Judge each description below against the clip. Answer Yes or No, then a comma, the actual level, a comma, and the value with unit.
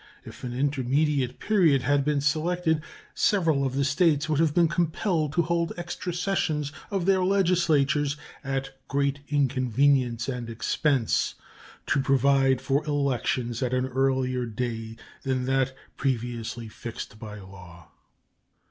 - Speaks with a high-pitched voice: No, medium, 140 Hz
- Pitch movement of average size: Yes, average, 3.5 semitones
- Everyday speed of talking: No, slow, 130 wpm